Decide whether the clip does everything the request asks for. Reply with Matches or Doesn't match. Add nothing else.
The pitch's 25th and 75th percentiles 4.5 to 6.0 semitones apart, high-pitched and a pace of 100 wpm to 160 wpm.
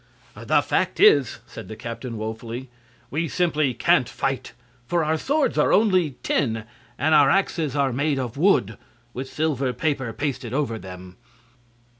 Doesn't match